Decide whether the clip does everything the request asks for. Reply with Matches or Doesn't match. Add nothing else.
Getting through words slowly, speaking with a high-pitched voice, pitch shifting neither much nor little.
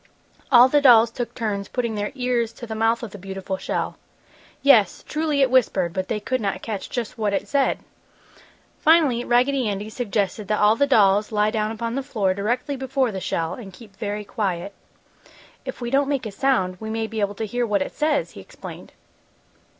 Doesn't match